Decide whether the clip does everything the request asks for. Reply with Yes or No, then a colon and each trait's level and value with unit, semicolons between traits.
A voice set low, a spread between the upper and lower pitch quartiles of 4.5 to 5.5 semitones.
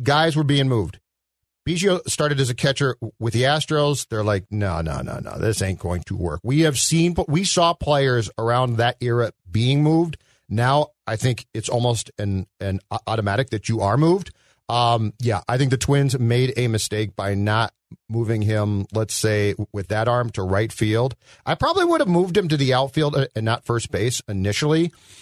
Yes: low, 120 Hz; average, 4.8 semitones